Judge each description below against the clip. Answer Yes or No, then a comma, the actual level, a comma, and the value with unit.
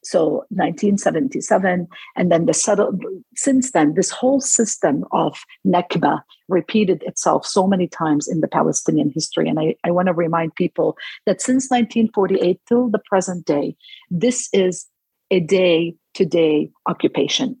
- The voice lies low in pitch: No, high, 190 Hz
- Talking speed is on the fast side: No, average, 145 wpm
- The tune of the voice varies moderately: No, wide, 6.1 semitones